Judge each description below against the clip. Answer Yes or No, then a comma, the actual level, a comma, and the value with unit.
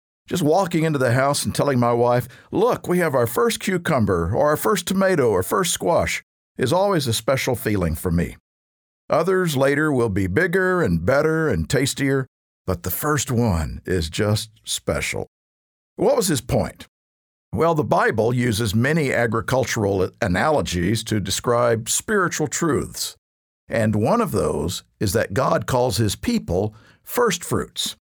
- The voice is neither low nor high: No, low, 120 Hz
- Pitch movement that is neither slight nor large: No, wide, 8.0 semitones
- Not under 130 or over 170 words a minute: Yes, average, 150 wpm